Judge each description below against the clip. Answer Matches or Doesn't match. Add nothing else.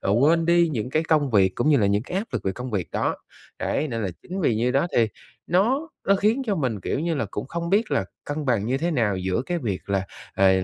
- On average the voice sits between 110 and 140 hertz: Matches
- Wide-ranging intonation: Matches